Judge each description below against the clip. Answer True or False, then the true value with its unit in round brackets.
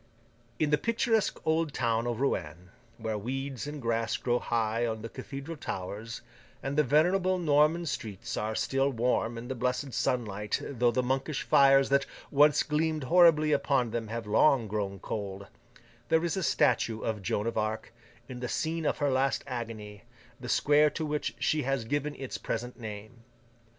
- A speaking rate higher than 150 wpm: True (170 wpm)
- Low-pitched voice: True (125 Hz)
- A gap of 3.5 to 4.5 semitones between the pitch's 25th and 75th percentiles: False (4.9 semitones)